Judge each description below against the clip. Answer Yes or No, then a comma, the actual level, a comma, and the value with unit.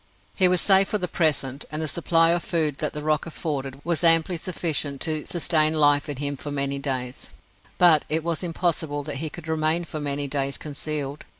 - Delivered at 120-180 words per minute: No, average, 200 wpm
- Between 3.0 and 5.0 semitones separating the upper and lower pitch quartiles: No, narrow, 2.6 semitones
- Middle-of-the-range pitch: Yes, medium, 155 Hz